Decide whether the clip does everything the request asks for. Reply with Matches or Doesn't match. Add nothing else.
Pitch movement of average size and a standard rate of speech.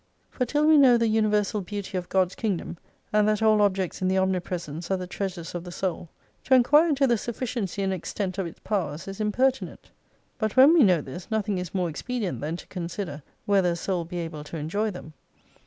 Doesn't match